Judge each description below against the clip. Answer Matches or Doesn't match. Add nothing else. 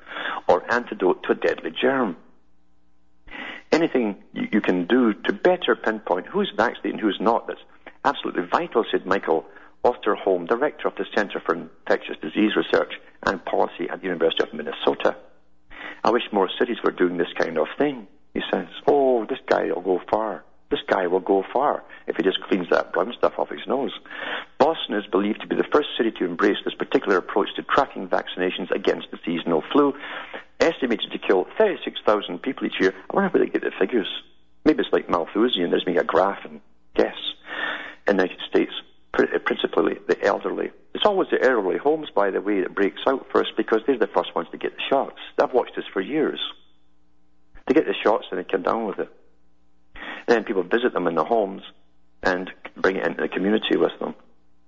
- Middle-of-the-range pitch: Doesn't match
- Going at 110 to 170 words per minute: Doesn't match